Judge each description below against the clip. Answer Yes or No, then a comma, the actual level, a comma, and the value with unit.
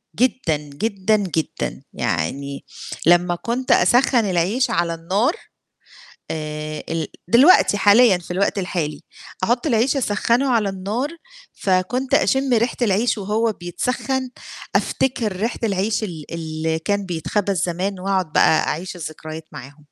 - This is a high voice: Yes, high, 195 Hz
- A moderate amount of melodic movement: No, wide, 5.9 semitones